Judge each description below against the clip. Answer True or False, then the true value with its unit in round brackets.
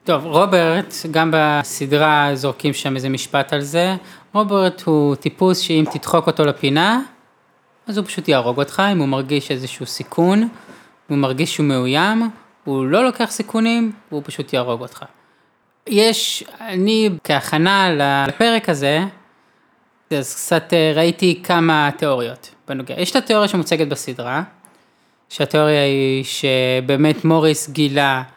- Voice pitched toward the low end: False (155 Hz)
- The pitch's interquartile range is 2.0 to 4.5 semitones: False (4.9 semitones)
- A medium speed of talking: True (125 wpm)